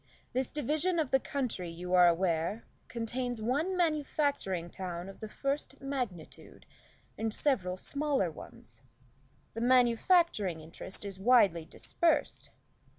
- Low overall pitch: No, high, 230 Hz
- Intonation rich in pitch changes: Yes, wide, 7.5 semitones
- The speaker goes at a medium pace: No, slow, 120 wpm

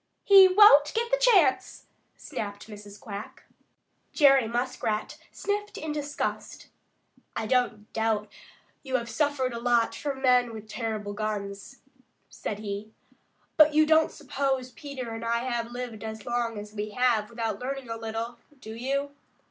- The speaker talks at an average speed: Yes, average, 150 wpm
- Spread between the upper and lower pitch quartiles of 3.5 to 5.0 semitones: Yes, average, 4.1 semitones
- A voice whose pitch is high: Yes, high, 240 Hz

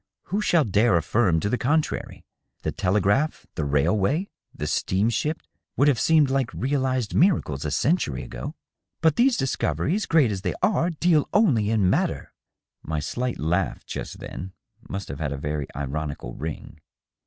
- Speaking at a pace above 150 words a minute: Yes, average, 160 wpm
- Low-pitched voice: Yes, low, 115 Hz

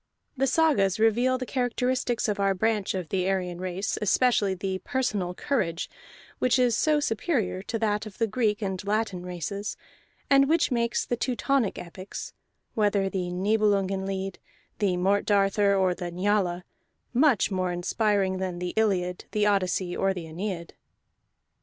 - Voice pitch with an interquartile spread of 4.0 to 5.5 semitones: No, average, 3.4 semitones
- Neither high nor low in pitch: No, high, 200 Hz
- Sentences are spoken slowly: No, average, 155 wpm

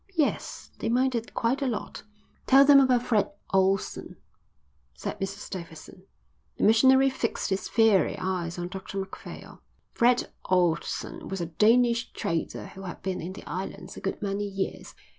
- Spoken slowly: No, average, 155 wpm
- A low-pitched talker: No, high, 200 Hz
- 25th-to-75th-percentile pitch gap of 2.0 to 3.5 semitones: No, average, 4.3 semitones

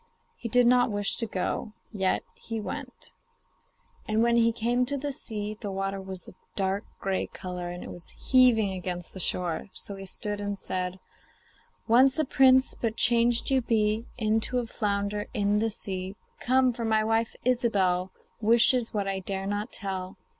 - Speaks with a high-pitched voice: Yes, high, 215 Hz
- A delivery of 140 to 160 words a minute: No, average, 170 wpm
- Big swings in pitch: No, average, 3.4 semitones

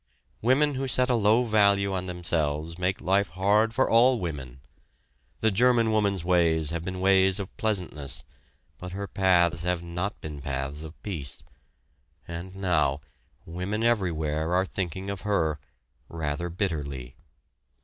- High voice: No, very low, 90 Hz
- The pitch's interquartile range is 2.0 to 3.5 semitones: No, average, 4.1 semitones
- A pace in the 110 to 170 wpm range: Yes, average, 140 wpm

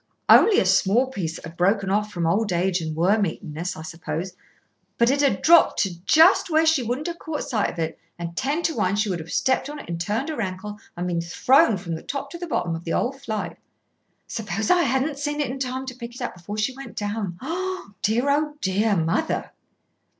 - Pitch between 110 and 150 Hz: No, high, 215 Hz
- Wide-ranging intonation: Yes, wide, 7.6 semitones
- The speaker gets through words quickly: Yes, fast, 225 wpm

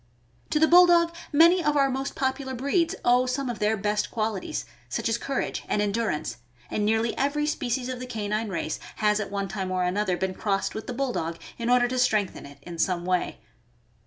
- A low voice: No, high, 230 Hz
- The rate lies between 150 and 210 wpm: Yes, average, 200 wpm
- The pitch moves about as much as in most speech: Yes, average, 5.0 semitones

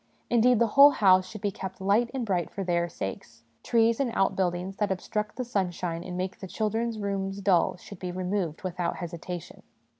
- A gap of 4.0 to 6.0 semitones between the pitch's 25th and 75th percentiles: No, average, 3.3 semitones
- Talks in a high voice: Yes, high, 195 Hz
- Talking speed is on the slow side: No, average, 185 wpm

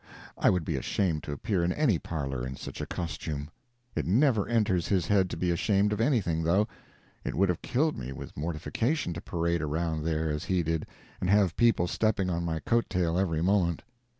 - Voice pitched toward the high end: No, very low, 85 Hz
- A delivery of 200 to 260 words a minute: Yes, fast, 205 wpm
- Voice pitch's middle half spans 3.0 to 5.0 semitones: Yes, average, 4.1 semitones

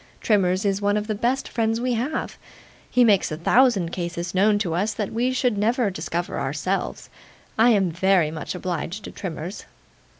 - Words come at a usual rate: Yes, average, 185 wpm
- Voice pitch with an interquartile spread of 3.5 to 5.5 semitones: Yes, average, 4.3 semitones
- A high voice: Yes, high, 200 Hz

